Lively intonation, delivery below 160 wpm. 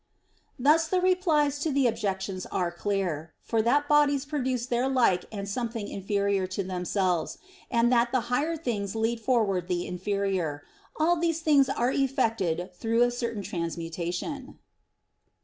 Yes: wide, 6.2 semitones; average, 145 wpm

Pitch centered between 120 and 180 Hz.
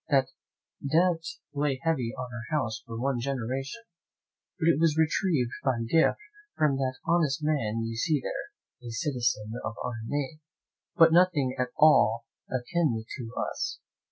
Yes: low, 135 Hz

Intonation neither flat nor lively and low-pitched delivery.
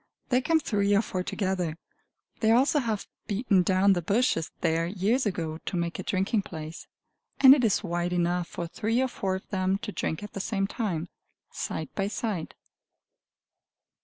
No: average, 4.0 semitones; high, 195 Hz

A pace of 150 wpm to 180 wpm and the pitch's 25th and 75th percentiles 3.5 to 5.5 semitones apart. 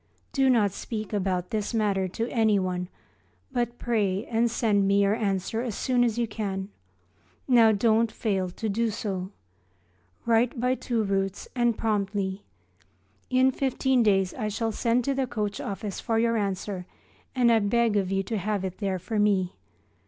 No: average, 165 wpm; average, 3.1 semitones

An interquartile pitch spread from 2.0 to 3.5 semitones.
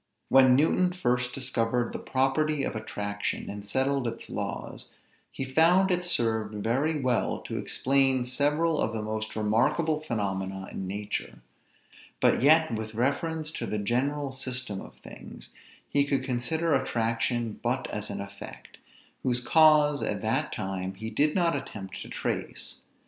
No: average, 5.1 semitones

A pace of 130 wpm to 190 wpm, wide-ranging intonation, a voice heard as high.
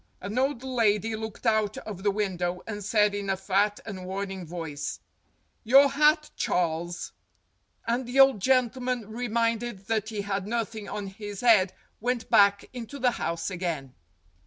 No: average, 155 wpm; average, 3.6 semitones; high, 210 Hz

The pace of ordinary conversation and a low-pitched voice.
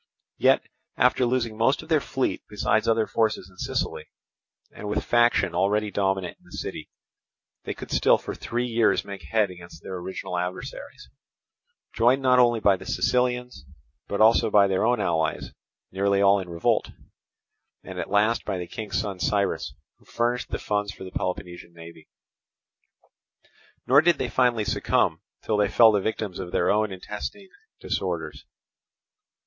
Yes: average, 160 wpm; low, 105 Hz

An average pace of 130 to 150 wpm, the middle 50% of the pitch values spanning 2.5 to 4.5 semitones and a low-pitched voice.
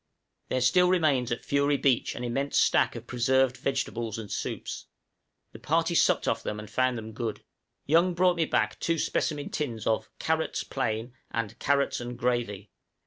No: average, 170 wpm; average, 3.8 semitones; low, 125 Hz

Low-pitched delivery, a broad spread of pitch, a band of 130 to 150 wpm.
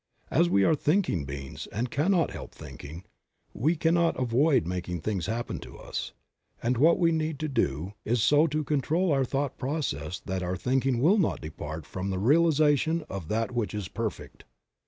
No: low, 125 Hz; wide, 8.6 semitones; average, 180 wpm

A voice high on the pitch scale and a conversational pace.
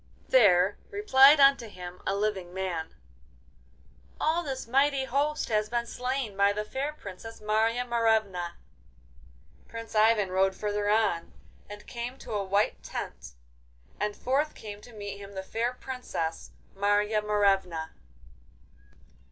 No: high, 215 Hz; slow, 130 wpm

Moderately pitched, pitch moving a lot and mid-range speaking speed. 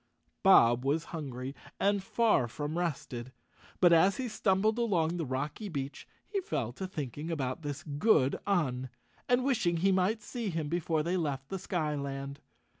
Yes: medium, 165 Hz; wide, 5.7 semitones; average, 165 wpm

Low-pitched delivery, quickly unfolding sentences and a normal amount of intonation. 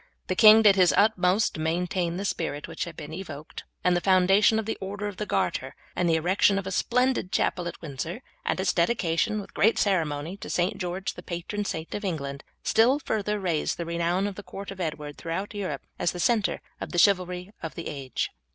No: medium, 185 Hz; fast, 215 wpm; average, 3.3 semitones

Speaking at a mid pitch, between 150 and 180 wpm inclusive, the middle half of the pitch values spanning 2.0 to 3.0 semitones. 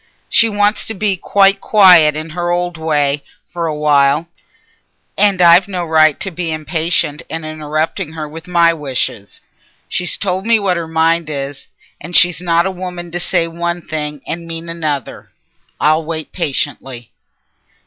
Yes: medium, 165 Hz; average, 160 wpm; narrow, 2.5 semitones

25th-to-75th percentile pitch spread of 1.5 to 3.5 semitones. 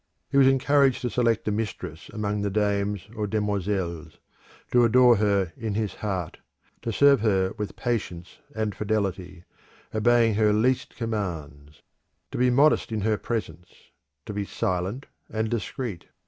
Yes: average, 3.1 semitones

